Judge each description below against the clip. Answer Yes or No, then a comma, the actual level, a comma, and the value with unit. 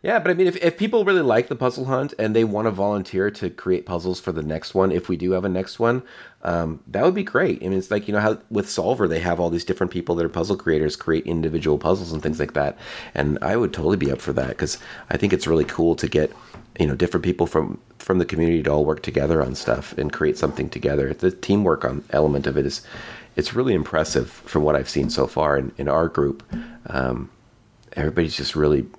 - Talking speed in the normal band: No, fast, 245 wpm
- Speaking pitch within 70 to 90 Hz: Yes, very low, 85 Hz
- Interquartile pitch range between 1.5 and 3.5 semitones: No, average, 4.4 semitones